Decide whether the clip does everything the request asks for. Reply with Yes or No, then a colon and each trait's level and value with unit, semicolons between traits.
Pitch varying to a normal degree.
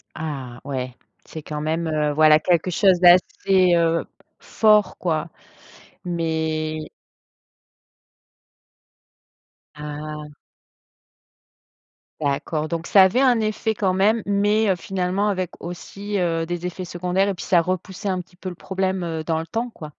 Yes: average, 3.4 semitones